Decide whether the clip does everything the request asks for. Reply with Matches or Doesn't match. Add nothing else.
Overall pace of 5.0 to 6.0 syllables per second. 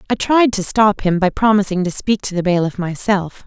Matches